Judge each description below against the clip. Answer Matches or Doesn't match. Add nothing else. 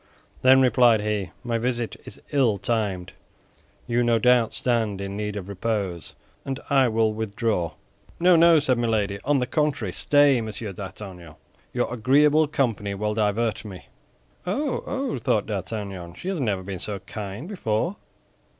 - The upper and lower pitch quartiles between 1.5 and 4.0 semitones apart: Doesn't match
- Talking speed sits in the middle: Matches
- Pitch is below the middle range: Matches